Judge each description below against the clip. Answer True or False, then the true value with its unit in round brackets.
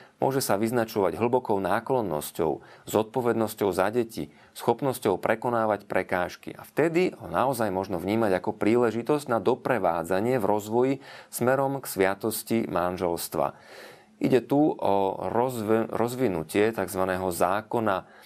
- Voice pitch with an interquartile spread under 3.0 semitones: False (4.4 semitones)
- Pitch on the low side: True (110 Hz)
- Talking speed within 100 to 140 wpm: True (110 wpm)